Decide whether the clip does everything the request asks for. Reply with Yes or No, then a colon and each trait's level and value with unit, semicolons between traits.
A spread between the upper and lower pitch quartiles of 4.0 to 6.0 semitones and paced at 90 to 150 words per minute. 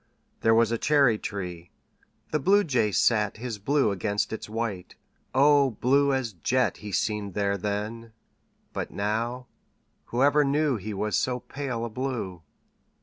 Yes: average, 4.3 semitones; average, 145 wpm